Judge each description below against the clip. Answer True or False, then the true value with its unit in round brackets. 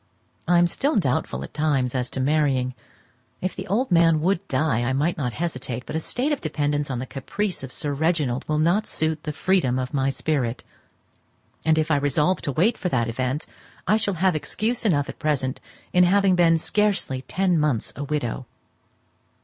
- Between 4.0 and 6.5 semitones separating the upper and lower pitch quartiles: True (5.2 semitones)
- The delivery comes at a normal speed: True (190 wpm)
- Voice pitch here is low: False (155 Hz)